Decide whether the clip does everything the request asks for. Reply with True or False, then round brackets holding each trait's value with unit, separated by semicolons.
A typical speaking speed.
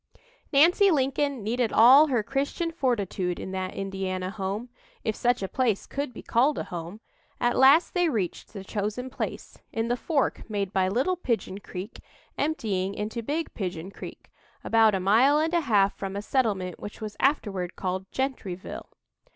True (165 wpm)